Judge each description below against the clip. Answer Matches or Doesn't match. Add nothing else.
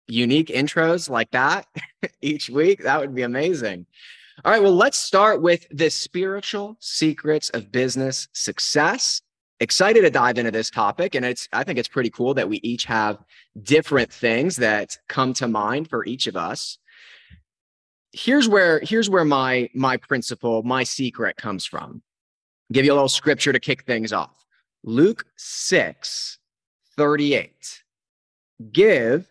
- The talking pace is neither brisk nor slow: Matches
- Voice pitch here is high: Doesn't match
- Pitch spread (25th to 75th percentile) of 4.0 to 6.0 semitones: Matches